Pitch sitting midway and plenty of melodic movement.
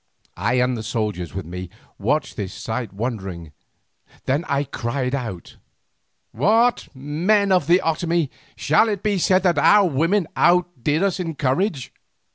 Yes: medium, 145 Hz; wide, 7.4 semitones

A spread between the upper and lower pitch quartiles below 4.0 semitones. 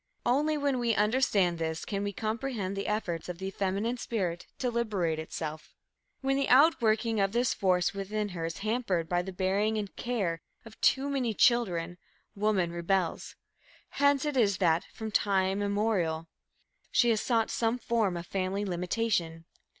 No: average, 4.6 semitones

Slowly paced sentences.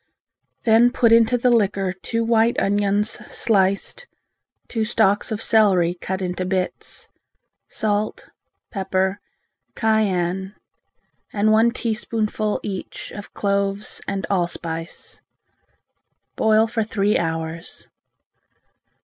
Yes: slow, 100 wpm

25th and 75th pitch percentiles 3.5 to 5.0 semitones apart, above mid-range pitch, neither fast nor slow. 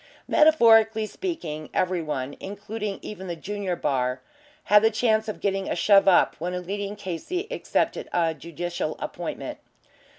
Yes: average, 4.2 semitones; high, 195 Hz; average, 145 wpm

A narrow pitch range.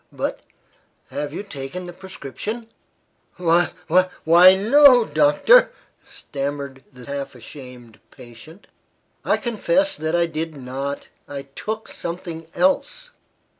No: average, 5.3 semitones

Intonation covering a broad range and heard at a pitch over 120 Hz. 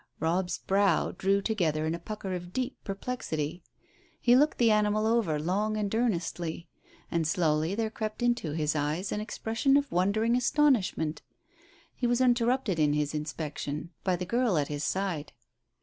Yes: wide, 6.1 semitones; high, 190 Hz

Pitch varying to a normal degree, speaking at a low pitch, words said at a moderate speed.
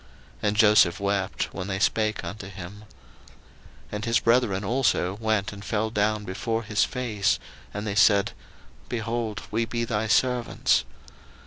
No: narrow, 2.2 semitones; low, 105 Hz; average, 145 wpm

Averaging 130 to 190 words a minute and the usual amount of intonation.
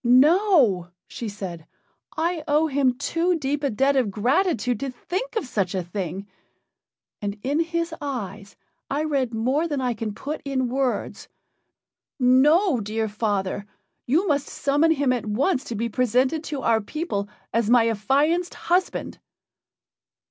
No: average, 150 wpm; wide, 5.8 semitones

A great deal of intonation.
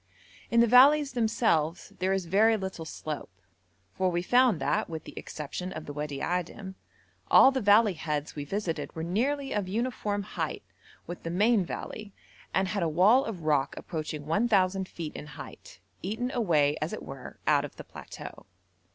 Yes: wide, 5.9 semitones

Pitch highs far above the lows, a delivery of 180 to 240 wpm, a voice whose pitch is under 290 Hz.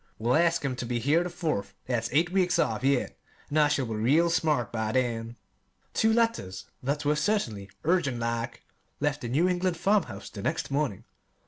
Yes: wide, 6.3 semitones; average, 190 wpm; medium, 140 Hz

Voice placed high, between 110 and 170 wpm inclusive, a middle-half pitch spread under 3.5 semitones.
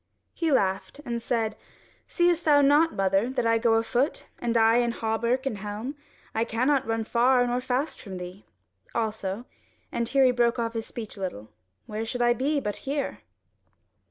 No: high, 235 Hz; average, 180 wpm; average, 2.9 semitones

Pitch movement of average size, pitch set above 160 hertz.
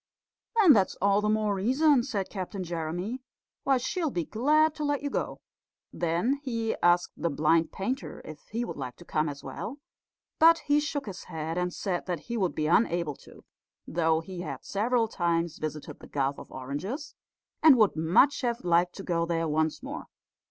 No: wide, 7.0 semitones; high, 190 Hz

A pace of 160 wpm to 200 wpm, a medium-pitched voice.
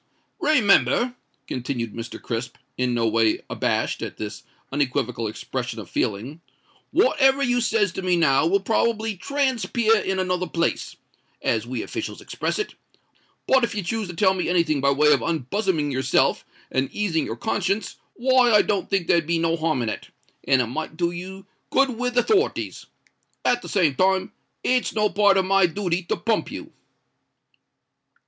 Yes: average, 170 wpm; medium, 180 Hz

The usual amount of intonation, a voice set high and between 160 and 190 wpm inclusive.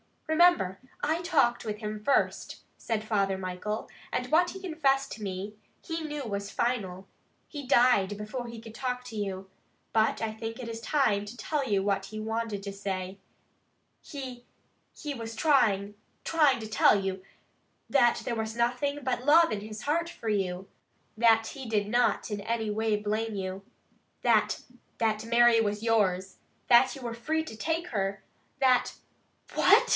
Yes: average, 4.3 semitones; high, 225 Hz; average, 170 wpm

